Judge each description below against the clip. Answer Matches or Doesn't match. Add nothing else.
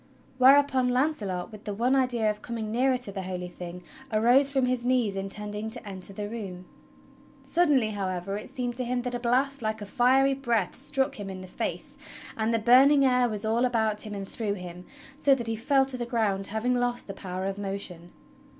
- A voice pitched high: Matches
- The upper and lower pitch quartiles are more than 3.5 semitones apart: Matches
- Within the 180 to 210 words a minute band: Matches